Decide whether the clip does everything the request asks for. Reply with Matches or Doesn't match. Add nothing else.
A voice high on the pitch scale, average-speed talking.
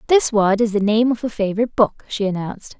Doesn't match